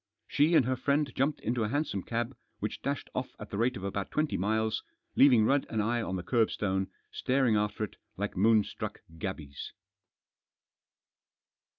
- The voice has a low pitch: Yes, low, 115 Hz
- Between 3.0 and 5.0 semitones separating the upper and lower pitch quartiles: Yes, average, 4.4 semitones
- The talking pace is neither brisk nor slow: Yes, average, 165 wpm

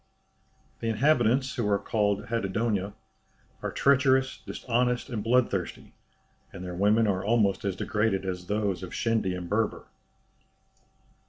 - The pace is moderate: No, slow, 130 wpm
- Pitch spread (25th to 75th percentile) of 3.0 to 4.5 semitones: Yes, average, 3.3 semitones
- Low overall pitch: Yes, low, 105 Hz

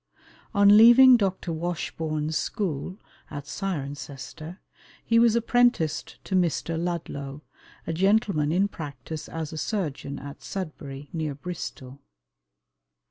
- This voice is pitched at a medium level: Yes, medium, 165 Hz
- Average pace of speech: No, slow, 110 wpm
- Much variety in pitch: No, average, 5.0 semitones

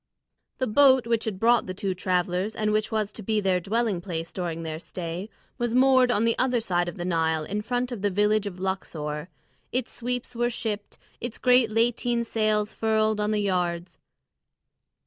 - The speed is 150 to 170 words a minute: No, average, 185 wpm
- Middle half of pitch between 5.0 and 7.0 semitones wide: No, average, 4.3 semitones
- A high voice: Yes, high, 210 Hz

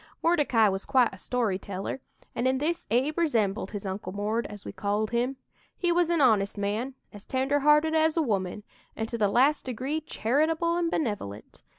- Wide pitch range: Yes, wide, 6.6 semitones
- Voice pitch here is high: Yes, high, 245 Hz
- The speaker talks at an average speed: Yes, average, 190 wpm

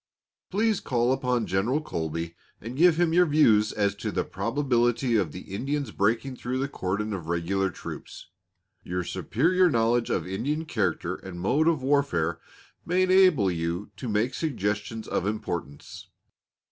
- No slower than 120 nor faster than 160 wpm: Yes, average, 150 wpm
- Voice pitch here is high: No, low, 115 Hz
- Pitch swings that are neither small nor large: No, wide, 7.0 semitones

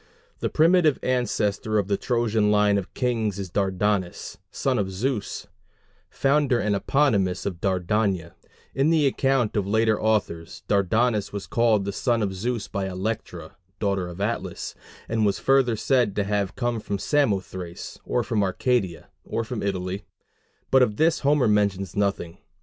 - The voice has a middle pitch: No, low, 105 Hz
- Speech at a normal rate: Yes, average, 155 wpm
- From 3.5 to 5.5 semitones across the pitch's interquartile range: Yes, average, 3.9 semitones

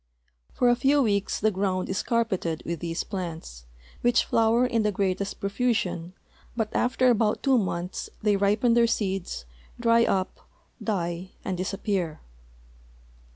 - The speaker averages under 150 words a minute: Yes, average, 140 wpm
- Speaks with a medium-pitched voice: No, high, 200 Hz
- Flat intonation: No, average, 4.1 semitones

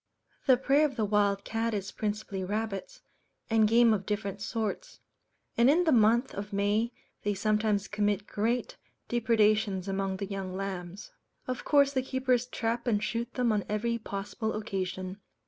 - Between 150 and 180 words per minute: Yes, average, 160 wpm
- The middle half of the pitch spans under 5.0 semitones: Yes, average, 2.9 semitones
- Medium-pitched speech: No, high, 215 Hz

